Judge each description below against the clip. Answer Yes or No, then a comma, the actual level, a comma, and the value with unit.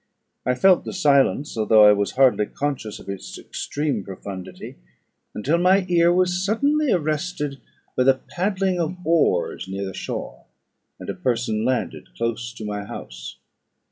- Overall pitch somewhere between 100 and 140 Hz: Yes, low, 135 Hz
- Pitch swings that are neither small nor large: No, wide, 8.8 semitones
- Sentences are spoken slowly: No, average, 150 wpm